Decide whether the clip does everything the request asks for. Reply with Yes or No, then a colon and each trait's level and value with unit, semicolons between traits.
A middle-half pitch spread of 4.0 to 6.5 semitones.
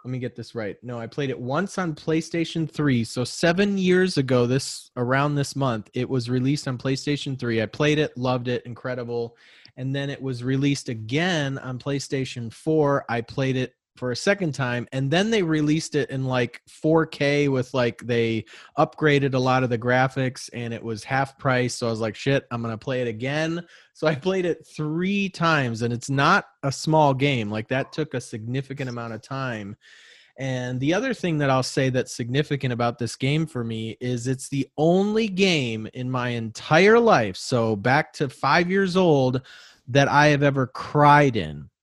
No: average, 3.5 semitones